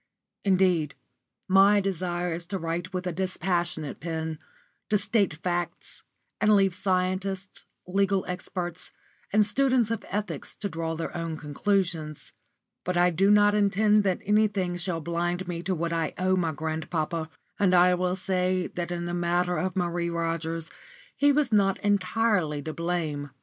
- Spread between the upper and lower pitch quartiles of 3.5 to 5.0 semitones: No, average, 2.7 semitones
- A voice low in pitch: No, medium, 180 Hz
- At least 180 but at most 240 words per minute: No, average, 155 wpm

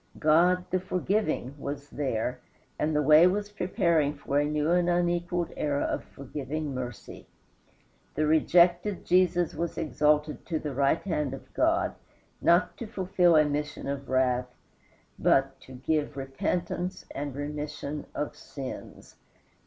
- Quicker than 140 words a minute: No, slow, 135 wpm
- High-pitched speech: No, medium, 150 Hz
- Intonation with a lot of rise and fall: No, average, 3.7 semitones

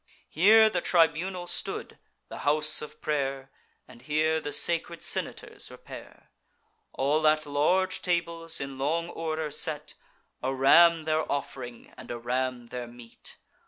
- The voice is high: No, medium, 155 Hz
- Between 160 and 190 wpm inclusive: No, slow, 135 wpm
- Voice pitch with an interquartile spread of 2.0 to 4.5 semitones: Yes, average, 3.7 semitones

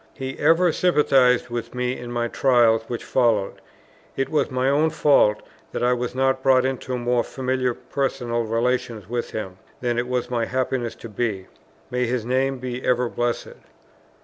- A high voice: No, low, 125 Hz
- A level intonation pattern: Yes, narrow, 1.8 semitones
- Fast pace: No, average, 170 wpm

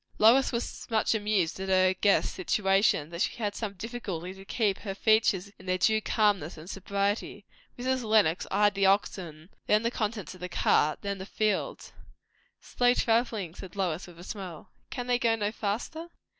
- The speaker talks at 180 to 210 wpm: Yes, average, 185 wpm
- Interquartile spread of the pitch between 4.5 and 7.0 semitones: No, average, 2.9 semitones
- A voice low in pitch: No, high, 200 Hz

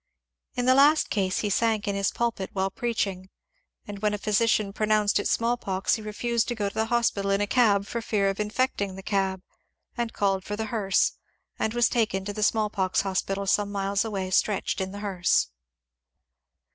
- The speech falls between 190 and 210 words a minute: Yes, average, 200 wpm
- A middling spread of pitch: No, narrow, 2.3 semitones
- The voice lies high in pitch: Yes, high, 205 Hz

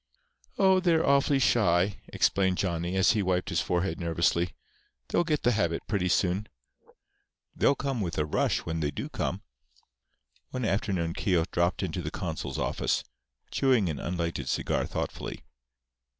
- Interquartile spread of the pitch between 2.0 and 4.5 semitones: No, wide, 5.4 semitones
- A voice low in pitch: Yes, very low, 95 Hz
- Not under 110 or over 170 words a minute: Yes, average, 150 wpm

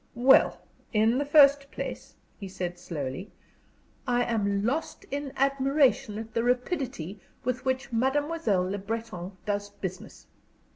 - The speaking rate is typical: No, slow, 130 wpm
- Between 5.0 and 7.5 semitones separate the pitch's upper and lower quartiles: Yes, wide, 5.4 semitones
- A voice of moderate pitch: No, high, 230 Hz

